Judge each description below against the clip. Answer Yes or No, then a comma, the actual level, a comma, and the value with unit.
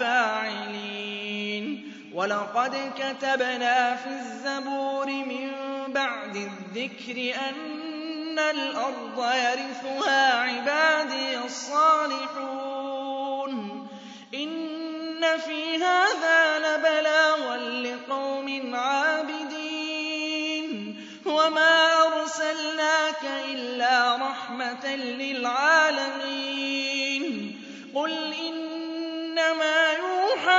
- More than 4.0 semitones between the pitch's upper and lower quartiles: No, average, 3.7 semitones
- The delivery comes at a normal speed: No, slow, 50 wpm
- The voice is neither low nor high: No, very high, 275 Hz